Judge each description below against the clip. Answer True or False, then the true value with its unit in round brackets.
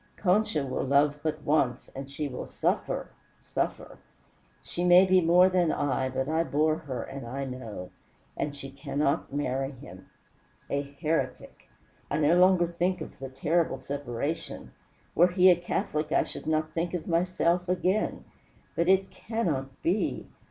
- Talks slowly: False (155 wpm)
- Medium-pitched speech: True (155 Hz)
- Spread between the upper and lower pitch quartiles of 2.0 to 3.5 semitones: False (4.3 semitones)